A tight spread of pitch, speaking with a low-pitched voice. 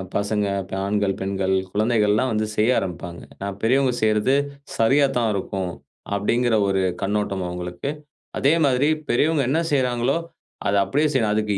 No: average, 4.4 semitones; low, 110 Hz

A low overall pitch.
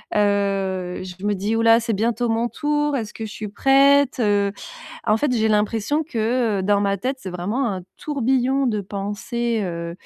No: high, 215 Hz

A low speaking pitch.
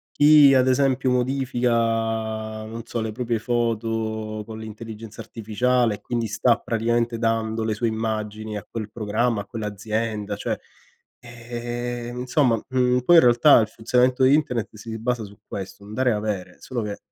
Yes: low, 115 Hz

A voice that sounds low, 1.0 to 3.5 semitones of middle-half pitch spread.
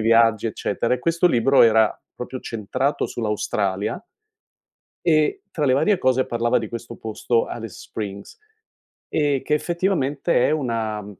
No: low, 120 Hz; average, 4.7 semitones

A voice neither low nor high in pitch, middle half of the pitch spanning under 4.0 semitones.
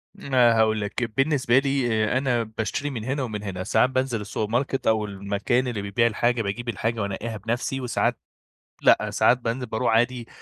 No: low, 115 Hz; average, 2.8 semitones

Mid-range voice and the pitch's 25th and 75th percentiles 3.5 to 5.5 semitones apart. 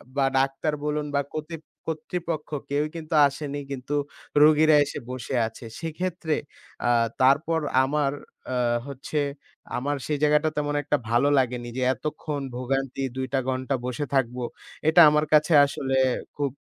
No: medium, 145 Hz; narrow, 2.4 semitones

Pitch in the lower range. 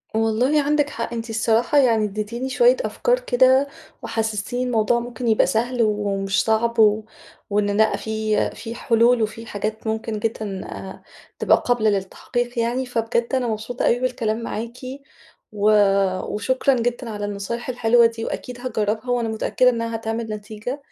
No: high, 230 Hz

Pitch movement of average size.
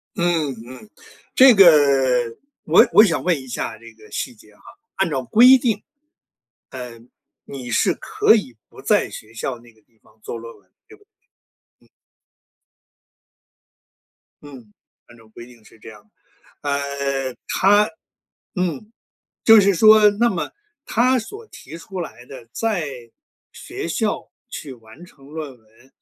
No: wide, 8.8 semitones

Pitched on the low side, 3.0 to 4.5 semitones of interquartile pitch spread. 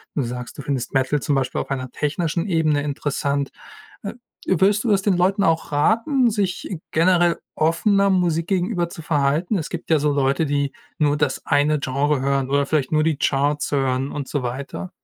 No: medium, 150 Hz; average, 4.0 semitones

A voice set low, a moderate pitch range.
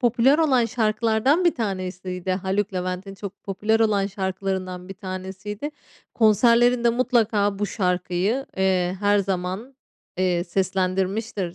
No: high, 195 Hz; average, 3.3 semitones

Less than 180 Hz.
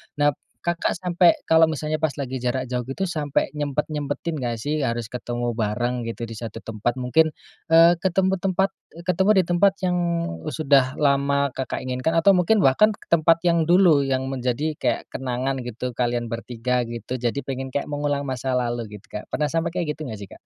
Yes: medium, 140 Hz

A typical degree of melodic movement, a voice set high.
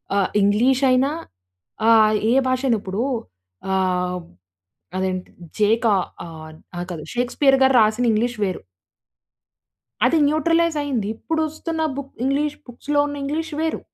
No: wide, 6.2 semitones; high, 245 Hz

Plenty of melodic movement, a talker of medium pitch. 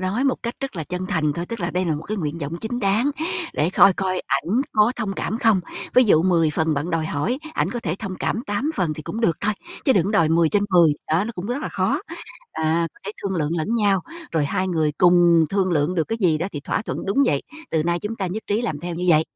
No: average, 4.6 semitones; medium, 180 Hz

